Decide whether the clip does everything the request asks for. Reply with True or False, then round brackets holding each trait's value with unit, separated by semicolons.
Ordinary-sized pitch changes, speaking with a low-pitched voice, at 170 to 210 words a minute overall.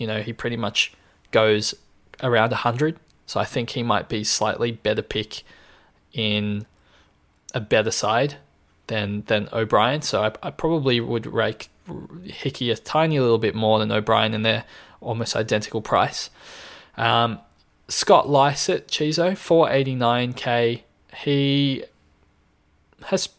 False (4.4 semitones; 115 Hz; 135 wpm)